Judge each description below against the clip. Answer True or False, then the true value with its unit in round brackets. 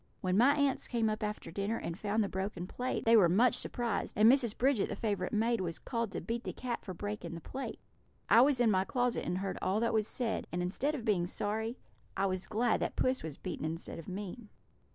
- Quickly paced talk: True (235 wpm)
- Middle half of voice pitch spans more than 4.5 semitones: False (4.2 semitones)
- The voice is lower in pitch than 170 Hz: False (215 Hz)